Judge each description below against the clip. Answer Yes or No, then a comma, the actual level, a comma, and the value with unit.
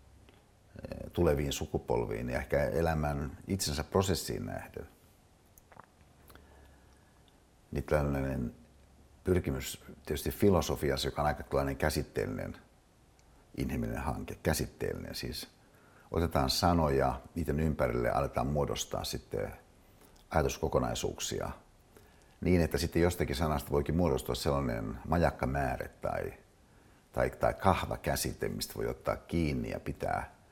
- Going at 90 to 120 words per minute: Yes, average, 100 wpm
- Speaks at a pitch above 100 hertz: No, very low, 75 Hz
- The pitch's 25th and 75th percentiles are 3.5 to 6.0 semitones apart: Yes, average, 3.9 semitones